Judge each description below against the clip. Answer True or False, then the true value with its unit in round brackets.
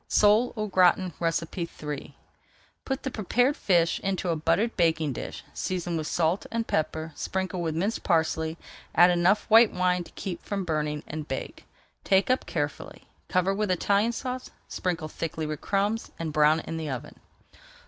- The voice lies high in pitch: False (175 Hz)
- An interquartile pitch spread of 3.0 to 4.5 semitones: True (4.0 semitones)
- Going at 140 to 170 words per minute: True (160 wpm)